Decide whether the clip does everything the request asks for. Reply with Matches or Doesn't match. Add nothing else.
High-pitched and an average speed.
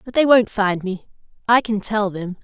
Doesn't match